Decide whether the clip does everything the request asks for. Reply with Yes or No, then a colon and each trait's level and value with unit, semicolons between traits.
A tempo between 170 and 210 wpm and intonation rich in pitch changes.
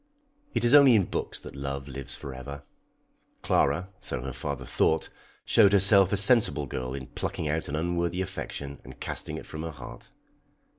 Yes: average, 185 wpm; wide, 6.0 semitones